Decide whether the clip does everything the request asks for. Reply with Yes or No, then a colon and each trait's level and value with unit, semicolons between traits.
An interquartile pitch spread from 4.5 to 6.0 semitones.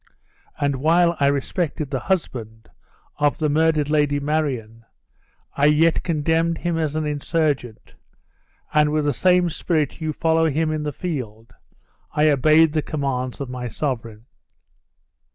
No: average, 2.9 semitones